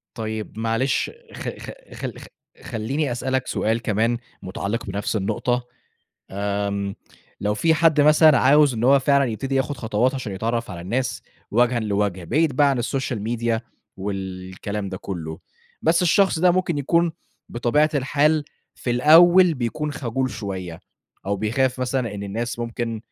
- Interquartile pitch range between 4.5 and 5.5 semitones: Yes, average, 5.2 semitones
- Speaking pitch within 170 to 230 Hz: No, low, 120 Hz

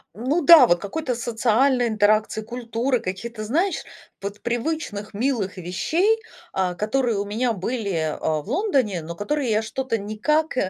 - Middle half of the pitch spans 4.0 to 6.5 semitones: Yes, average, 4.6 semitones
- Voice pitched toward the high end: Yes, high, 230 Hz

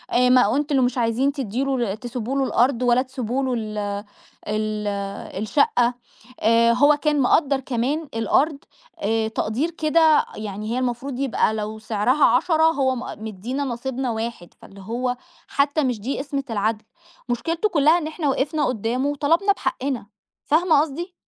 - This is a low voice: No, very high, 255 Hz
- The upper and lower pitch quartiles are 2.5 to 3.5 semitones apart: No, average, 4.2 semitones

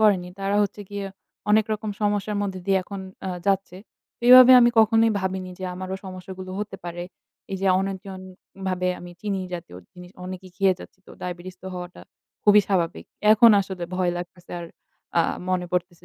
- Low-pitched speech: No, high, 190 Hz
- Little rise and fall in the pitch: Yes, narrow, 2.1 semitones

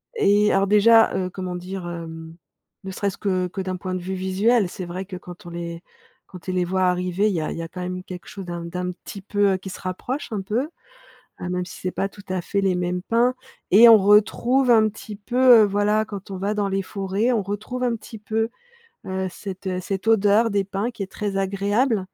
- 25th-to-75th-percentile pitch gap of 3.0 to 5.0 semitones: No, narrow, 2.4 semitones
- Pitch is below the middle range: No, high, 195 Hz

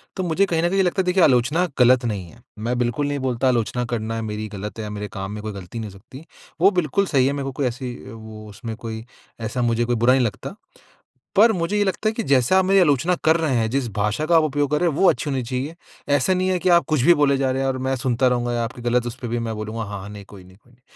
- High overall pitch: No, low, 125 Hz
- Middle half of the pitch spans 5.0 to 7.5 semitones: Yes, wide, 5.5 semitones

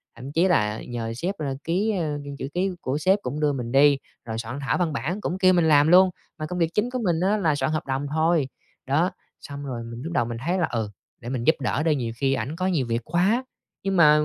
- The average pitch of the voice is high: No, medium, 150 Hz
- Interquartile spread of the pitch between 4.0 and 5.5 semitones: Yes, average, 5.1 semitones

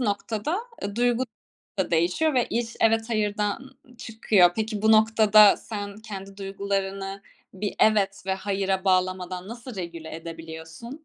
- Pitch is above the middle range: Yes, high, 200 Hz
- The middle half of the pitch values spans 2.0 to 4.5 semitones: Yes, average, 2.7 semitones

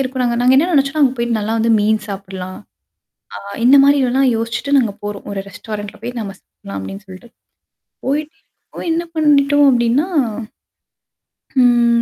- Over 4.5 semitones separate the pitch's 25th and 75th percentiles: Yes, average, 4.9 semitones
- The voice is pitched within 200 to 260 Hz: Yes, high, 235 Hz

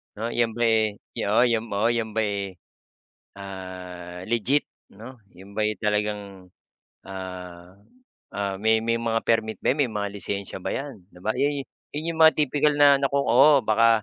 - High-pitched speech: No, low, 110 Hz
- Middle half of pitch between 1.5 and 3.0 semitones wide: No, average, 3.5 semitones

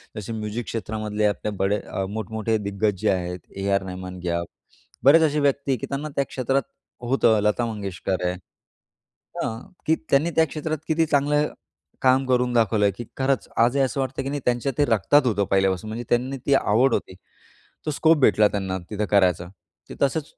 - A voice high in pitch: No, low, 115 Hz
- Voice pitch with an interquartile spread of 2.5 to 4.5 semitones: No, average, 5.2 semitones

